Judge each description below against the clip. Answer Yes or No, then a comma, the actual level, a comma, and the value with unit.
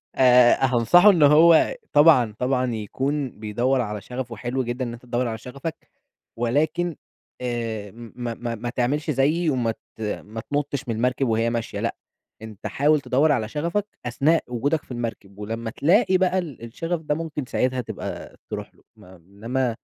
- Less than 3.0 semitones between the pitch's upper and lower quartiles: No, average, 4.2 semitones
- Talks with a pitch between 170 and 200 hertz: No, low, 125 Hz